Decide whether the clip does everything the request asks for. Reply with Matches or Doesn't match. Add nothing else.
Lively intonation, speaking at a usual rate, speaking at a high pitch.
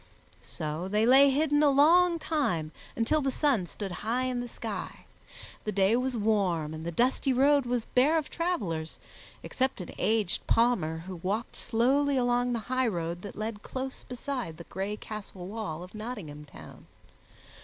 Matches